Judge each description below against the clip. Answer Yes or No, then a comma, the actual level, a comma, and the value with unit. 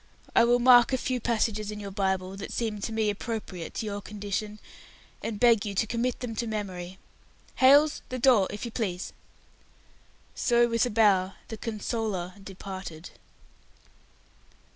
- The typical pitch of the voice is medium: No, high, 215 Hz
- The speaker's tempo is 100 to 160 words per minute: Yes, average, 155 wpm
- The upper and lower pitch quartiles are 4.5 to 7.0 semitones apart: No, average, 3.2 semitones